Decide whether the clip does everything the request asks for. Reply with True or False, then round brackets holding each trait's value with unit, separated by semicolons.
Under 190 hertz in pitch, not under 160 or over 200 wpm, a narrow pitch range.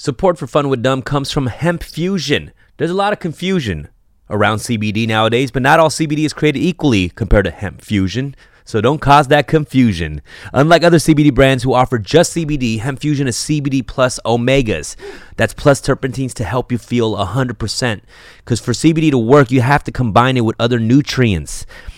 False (135 Hz; 185 wpm; 4.6 semitones)